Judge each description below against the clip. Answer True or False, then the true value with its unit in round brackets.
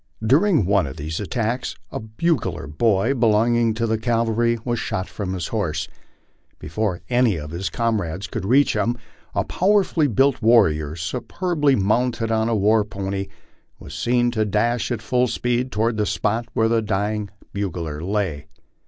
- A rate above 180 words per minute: False (160 wpm)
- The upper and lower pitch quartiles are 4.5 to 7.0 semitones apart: False (3.6 semitones)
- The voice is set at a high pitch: False (110 Hz)